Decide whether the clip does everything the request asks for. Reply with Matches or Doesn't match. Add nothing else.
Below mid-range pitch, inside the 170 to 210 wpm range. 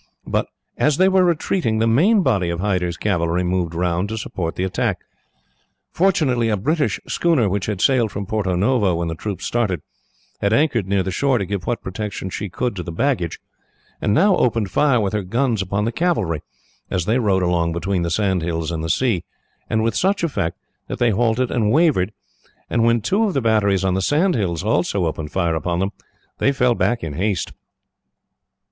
Matches